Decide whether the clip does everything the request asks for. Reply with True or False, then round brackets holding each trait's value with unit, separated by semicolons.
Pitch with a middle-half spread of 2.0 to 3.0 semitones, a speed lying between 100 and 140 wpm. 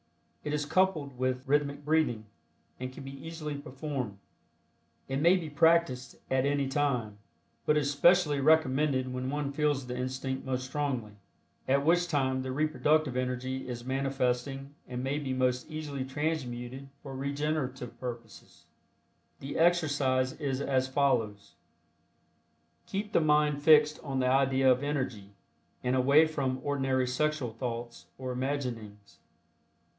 True (2.6 semitones; 135 wpm)